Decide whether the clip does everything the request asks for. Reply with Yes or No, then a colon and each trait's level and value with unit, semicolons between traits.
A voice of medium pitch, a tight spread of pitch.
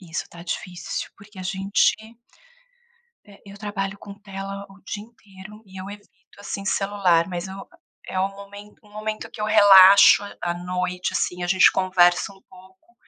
No: high, 195 Hz; narrow, 1.7 semitones